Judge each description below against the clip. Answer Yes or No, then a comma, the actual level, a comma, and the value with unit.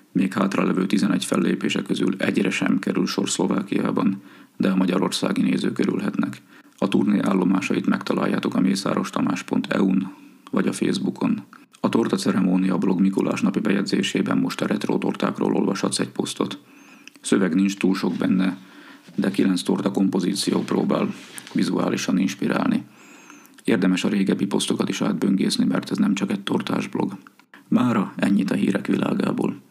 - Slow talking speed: No, average, 140 wpm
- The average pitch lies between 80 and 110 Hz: Yes, very low, 95 Hz